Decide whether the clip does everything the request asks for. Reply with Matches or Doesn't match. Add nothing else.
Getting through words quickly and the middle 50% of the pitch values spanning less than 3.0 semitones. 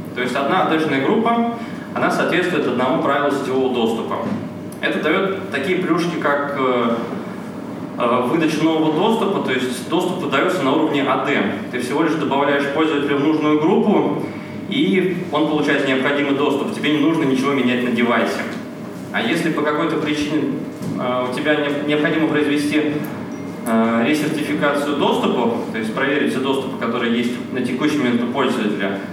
Doesn't match